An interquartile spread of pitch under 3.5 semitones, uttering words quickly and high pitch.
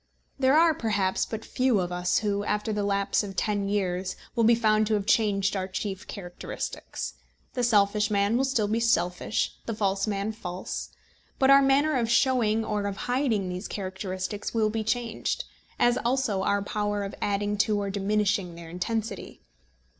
No: narrow, 2.5 semitones; average, 175 wpm; high, 210 Hz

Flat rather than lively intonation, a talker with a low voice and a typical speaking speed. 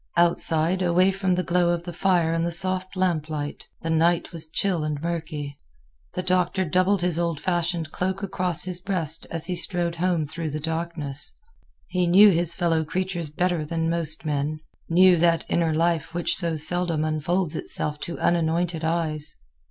No: narrow, 2.1 semitones; medium, 170 Hz; average, 170 wpm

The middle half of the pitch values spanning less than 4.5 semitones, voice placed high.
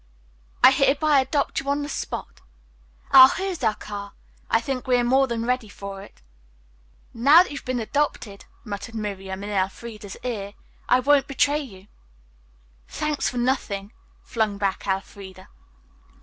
No: average, 5.2 semitones; high, 235 Hz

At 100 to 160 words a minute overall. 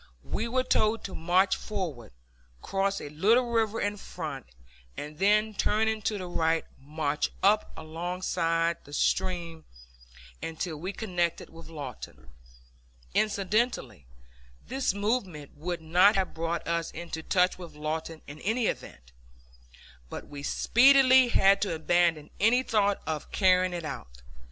Yes: slow, 135 wpm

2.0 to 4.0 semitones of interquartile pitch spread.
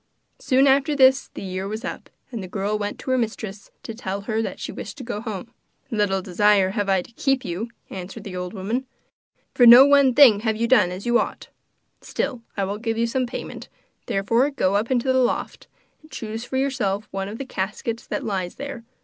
No: average, 4.5 semitones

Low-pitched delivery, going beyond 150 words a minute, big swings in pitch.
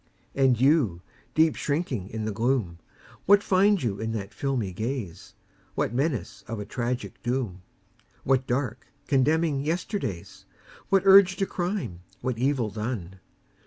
No: low, 130 Hz; slow, 135 wpm; wide, 6.3 semitones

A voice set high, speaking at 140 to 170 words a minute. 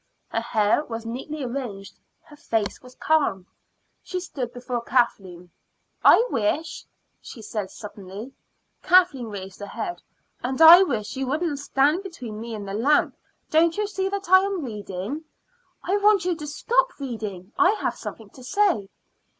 Yes: very high, 260 Hz; average, 160 wpm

